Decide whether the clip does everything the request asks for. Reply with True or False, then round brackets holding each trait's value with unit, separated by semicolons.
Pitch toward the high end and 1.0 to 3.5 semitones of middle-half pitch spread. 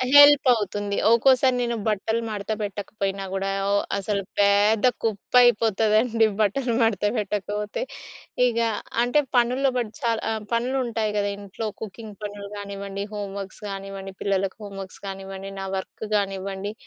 True (210 Hz; 2.7 semitones)